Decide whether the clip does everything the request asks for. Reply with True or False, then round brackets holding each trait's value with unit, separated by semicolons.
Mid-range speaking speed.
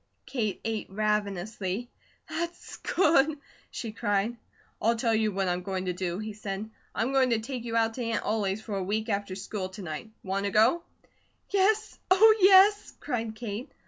True (175 wpm)